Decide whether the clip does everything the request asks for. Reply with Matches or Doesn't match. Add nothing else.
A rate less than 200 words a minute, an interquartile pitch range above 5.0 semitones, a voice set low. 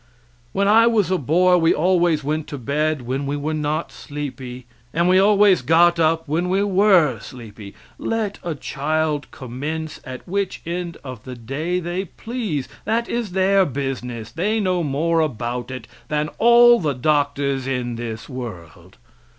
Doesn't match